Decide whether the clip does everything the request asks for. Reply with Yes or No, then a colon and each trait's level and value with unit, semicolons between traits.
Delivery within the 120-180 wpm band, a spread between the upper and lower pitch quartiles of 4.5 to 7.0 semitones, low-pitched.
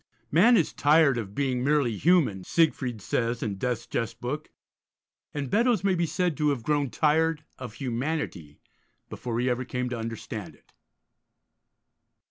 Yes: average, 150 wpm; average, 5.0 semitones; low, 130 Hz